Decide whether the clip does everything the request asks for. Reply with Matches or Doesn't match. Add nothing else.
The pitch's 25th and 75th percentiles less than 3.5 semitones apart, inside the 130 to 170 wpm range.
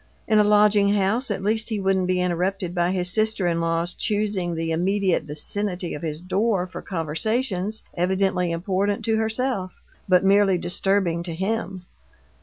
Matches